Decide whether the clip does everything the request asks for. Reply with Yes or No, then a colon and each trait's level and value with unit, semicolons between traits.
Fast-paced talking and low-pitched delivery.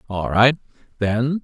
No: slow, 125 wpm; low, 120 Hz